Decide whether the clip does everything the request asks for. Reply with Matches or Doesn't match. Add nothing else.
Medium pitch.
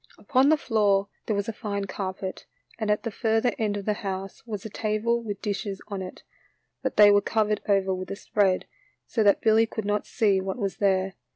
Doesn't match